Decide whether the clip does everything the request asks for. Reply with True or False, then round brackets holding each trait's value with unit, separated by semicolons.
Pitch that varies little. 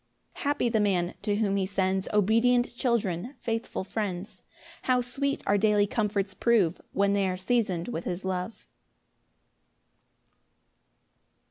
False (3.8 semitones)